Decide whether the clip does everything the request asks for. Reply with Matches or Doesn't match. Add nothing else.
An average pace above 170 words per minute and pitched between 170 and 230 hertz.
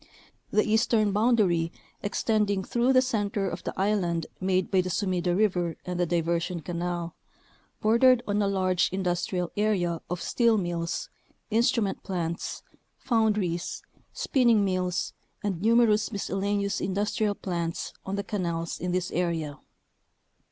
Doesn't match